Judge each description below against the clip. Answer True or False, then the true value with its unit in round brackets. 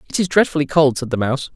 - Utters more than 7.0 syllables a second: True (7.3 syllables/s)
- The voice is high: False (140 Hz)